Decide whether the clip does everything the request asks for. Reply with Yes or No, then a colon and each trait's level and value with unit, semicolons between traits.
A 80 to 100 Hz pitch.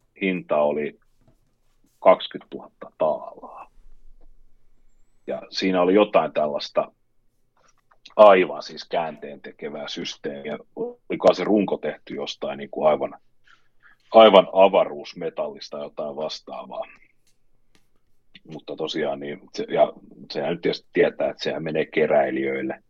Yes: very low, 90 Hz